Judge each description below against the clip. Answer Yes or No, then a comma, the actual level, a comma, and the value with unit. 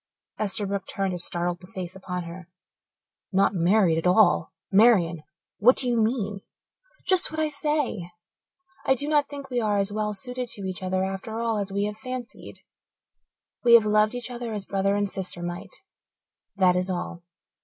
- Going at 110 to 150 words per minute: No, average, 175 wpm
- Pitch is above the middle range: Yes, high, 205 Hz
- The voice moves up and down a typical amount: Yes, average, 4.2 semitones